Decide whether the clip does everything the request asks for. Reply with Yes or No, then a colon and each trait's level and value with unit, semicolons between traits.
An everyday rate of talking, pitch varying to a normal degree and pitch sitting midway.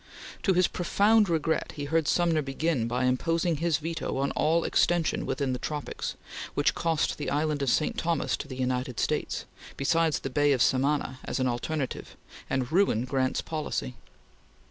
Yes: average, 165 wpm; average, 4.0 semitones; medium, 150 Hz